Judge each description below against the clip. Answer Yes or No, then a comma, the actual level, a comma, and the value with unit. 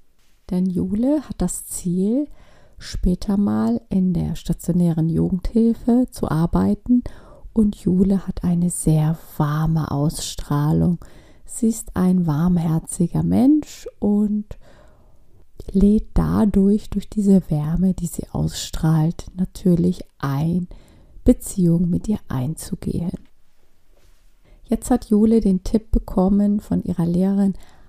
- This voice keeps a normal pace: No, slow, 105 wpm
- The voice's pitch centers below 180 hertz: No, medium, 185 Hz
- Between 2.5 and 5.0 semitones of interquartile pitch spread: Yes, average, 4.4 semitones